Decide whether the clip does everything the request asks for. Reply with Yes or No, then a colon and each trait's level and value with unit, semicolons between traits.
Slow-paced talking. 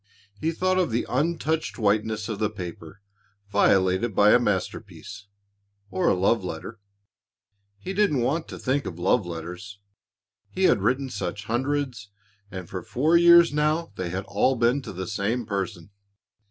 No: average, 155 wpm